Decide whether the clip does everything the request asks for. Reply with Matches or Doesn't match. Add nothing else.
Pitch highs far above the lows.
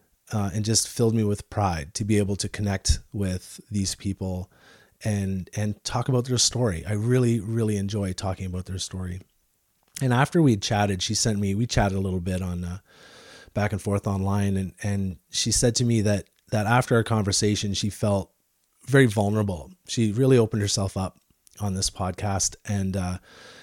Doesn't match